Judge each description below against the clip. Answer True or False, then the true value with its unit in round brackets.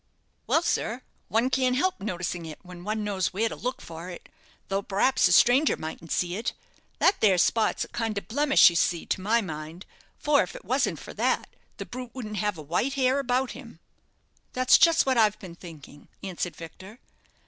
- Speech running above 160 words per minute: True (200 wpm)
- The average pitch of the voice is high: True (210 Hz)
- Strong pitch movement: True (6.2 semitones)